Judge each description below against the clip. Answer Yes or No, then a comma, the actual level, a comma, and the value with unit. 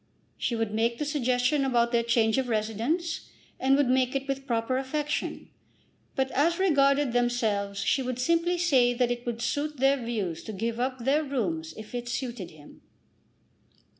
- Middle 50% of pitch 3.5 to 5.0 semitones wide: No, average, 3.1 semitones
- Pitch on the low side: No, high, 245 Hz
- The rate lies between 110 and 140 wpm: No, average, 170 wpm